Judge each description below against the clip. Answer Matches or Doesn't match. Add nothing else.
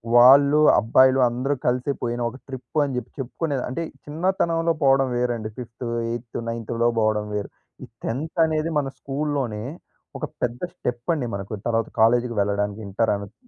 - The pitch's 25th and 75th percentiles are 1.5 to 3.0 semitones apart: Doesn't match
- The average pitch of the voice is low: Matches